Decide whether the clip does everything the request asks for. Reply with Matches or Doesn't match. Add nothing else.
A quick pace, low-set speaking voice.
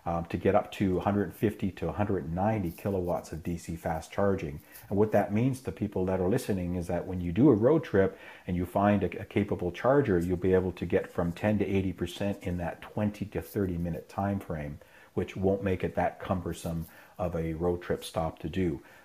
Matches